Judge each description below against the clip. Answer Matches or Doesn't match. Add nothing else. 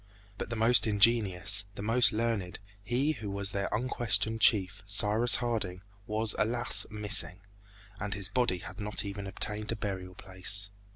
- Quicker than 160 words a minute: Doesn't match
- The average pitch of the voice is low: Matches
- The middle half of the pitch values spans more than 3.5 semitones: Doesn't match